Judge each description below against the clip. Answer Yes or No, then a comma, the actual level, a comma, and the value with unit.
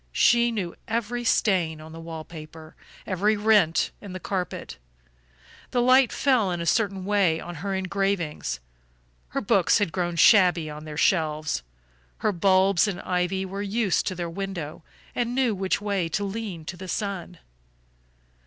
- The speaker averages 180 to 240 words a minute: No, average, 160 wpm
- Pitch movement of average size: Yes, average, 3.5 semitones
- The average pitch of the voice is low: No, high, 190 Hz